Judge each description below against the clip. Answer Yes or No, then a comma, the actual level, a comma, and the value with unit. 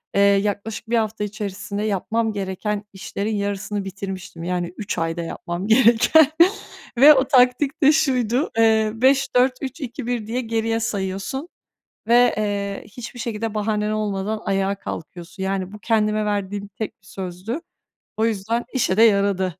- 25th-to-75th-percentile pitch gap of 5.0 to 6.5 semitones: No, average, 3.1 semitones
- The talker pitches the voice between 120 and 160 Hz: No, high, 210 Hz